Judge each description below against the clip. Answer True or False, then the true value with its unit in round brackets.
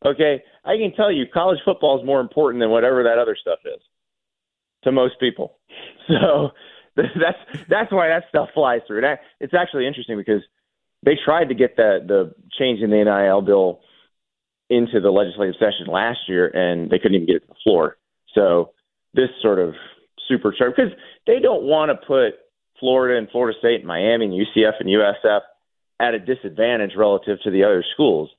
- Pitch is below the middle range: True (125 Hz)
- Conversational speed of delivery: True (185 wpm)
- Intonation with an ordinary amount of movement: False (6.6 semitones)